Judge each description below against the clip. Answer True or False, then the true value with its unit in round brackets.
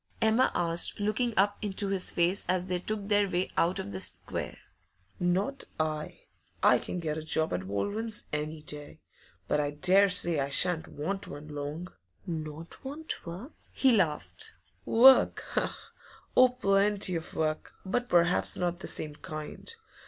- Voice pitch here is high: False (180 Hz)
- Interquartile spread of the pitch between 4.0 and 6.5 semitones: True (4.9 semitones)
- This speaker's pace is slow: False (155 wpm)